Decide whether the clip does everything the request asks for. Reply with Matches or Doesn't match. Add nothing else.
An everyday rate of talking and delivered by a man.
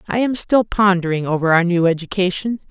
Doesn't match